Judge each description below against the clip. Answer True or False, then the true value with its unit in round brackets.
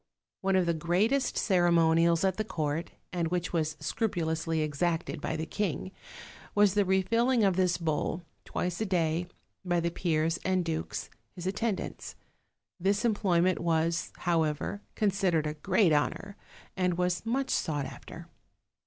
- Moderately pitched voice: True (175 Hz)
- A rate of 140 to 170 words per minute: True (145 wpm)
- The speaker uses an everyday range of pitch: True (3.0 semitones)